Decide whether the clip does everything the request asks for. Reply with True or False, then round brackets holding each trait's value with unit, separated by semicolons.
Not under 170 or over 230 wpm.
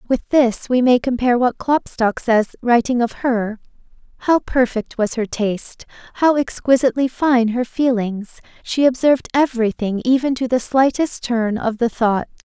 False (155 wpm)